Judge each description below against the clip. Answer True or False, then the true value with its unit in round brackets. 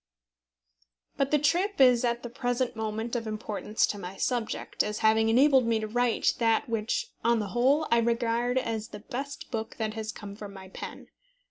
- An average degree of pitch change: False (2.3 semitones)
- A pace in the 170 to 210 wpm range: True (190 wpm)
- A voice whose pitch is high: True (230 Hz)